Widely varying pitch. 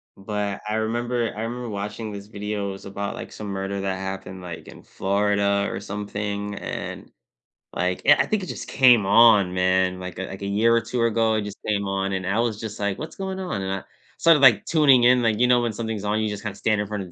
No: average, 2.9 semitones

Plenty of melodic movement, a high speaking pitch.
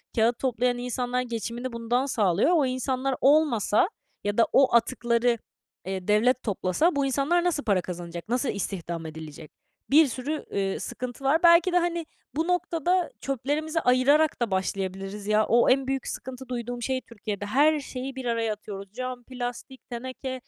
No: average, 4.3 semitones; very high, 250 Hz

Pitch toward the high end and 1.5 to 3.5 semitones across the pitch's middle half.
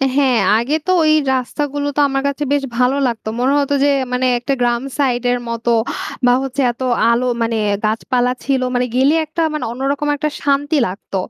Yes: very high, 260 Hz; average, 2.7 semitones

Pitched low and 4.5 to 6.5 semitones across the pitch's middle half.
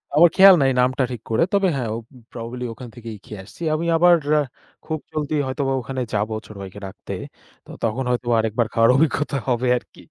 Yes: low, 125 Hz; average, 4.8 semitones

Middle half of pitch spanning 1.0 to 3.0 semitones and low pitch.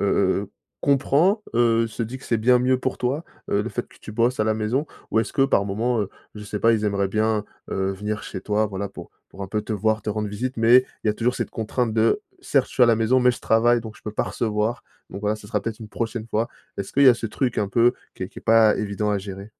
Yes: narrow, 2.6 semitones; low, 110 Hz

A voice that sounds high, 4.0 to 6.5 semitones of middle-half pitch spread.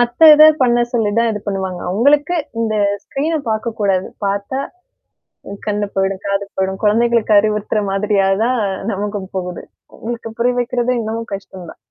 No: high, 215 Hz; average, 3.3 semitones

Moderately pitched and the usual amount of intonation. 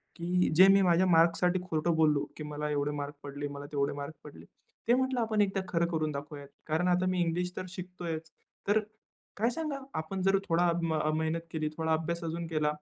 Yes: medium, 165 Hz; average, 3.0 semitones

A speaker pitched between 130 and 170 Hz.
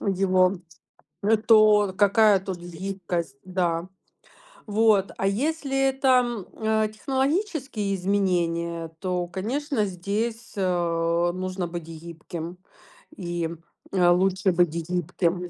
No: medium, 185 Hz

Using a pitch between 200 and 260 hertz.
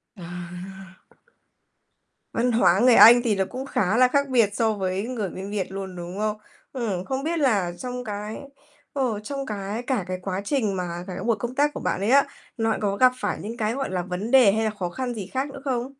Yes: high, 215 Hz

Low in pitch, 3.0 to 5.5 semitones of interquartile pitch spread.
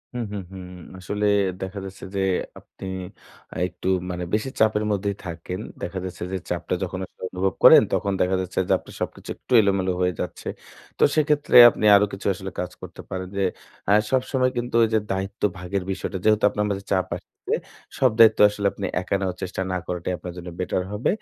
No: very low, 95 Hz; narrow, 2.5 semitones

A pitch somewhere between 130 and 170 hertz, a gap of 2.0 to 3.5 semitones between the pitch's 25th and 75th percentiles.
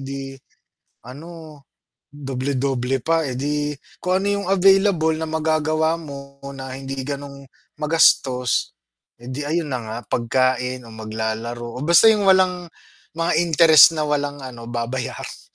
No: medium, 140 Hz; average, 3.9 semitones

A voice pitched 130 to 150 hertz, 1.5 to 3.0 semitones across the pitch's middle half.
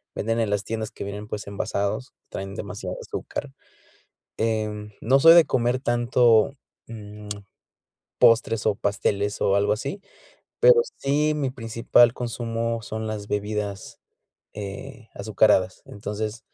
No: low, 110 Hz; narrow, 2.6 semitones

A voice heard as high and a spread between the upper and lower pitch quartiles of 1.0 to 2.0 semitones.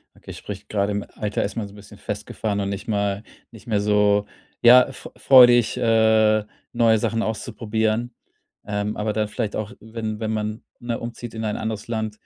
No: low, 110 Hz; narrow, 1.6 semitones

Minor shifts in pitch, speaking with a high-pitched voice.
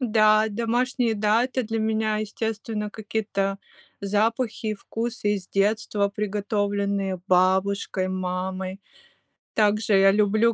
Yes: narrow, 2.0 semitones; high, 210 Hz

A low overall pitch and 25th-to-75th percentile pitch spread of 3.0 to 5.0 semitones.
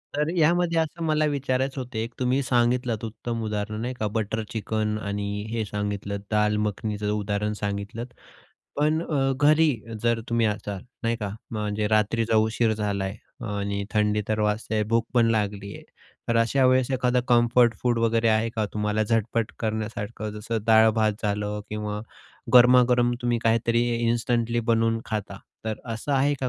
No: low, 115 Hz; narrow, 2.5 semitones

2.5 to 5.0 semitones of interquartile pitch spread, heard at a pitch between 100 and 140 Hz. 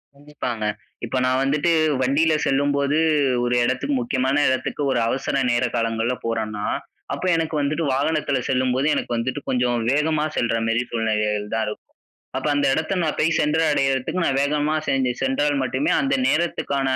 Yes: average, 3.4 semitones; low, 135 Hz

